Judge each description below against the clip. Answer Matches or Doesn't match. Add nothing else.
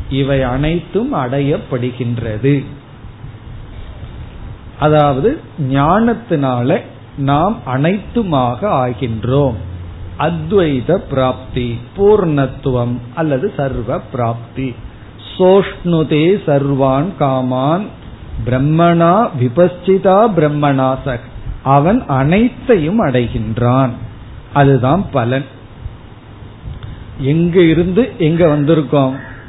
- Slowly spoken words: Matches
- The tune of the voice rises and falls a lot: Doesn't match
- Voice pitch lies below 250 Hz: Matches